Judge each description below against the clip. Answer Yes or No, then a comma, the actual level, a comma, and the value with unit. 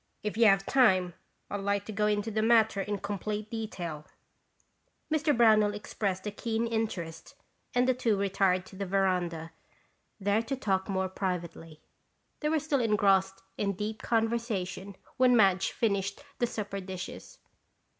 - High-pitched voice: Yes, high, 205 Hz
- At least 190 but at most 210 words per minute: No, average, 155 wpm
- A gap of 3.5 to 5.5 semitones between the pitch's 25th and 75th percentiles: No, average, 2.9 semitones